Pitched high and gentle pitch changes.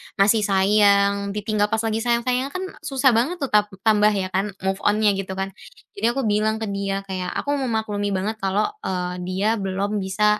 Yes: high, 210 Hz; narrow, 2.2 semitones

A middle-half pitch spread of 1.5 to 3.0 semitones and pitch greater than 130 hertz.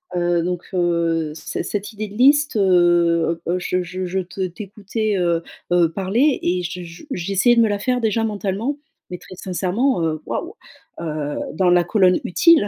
No: average, 3.7 semitones; medium, 185 Hz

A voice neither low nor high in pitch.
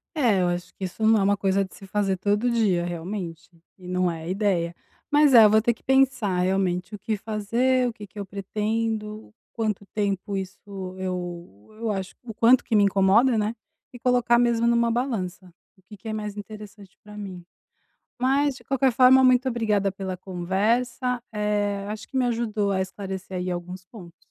No: high, 210 Hz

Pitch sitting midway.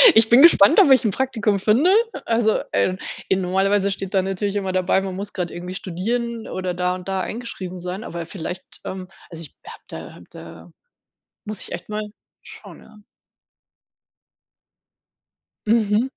No: high, 195 Hz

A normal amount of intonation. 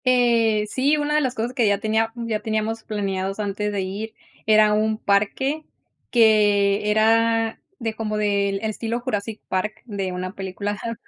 No: narrow, 2.0 semitones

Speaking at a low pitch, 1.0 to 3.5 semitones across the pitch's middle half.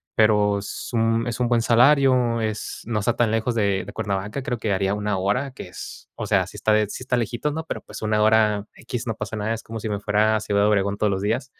Yes: low, 110 Hz; narrow, 2.5 semitones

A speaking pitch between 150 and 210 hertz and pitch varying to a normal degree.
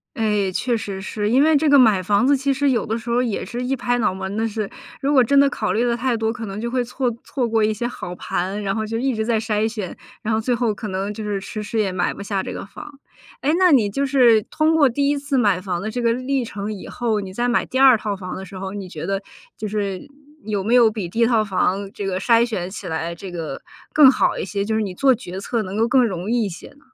No: high, 220 Hz; average, 3.8 semitones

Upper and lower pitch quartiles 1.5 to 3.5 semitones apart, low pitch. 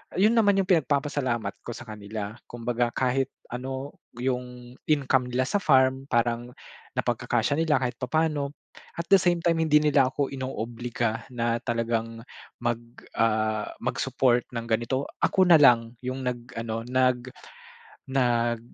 Yes: average, 3.0 semitones; low, 125 Hz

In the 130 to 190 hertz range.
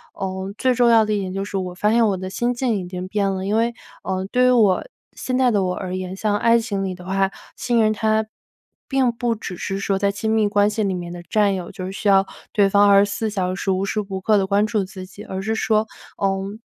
No: high, 200 Hz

